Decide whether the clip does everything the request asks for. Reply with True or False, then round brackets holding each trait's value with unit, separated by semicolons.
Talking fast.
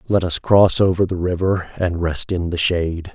True (210 wpm)